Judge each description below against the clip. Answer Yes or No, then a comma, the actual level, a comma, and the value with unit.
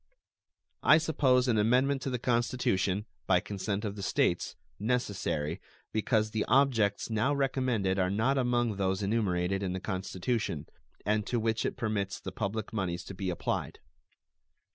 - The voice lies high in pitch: No, low, 105 Hz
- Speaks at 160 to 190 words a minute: No, average, 150 wpm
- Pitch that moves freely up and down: No, average, 4.3 semitones